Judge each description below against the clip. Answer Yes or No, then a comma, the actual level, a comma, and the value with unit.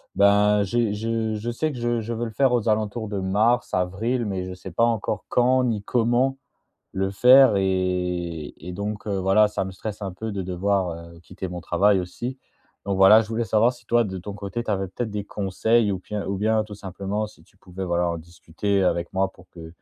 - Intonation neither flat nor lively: Yes, average, 3.2 semitones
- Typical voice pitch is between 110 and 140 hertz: No, low, 100 Hz